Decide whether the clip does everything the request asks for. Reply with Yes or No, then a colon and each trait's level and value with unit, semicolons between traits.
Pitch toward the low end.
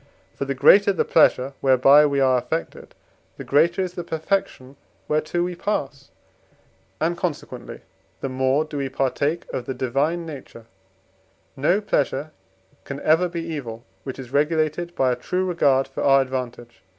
No: medium, 145 Hz